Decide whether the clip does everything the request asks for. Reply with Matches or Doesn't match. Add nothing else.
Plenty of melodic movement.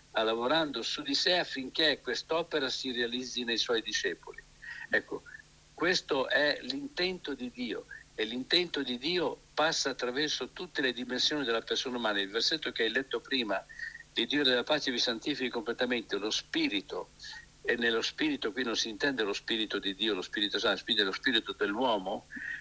Matches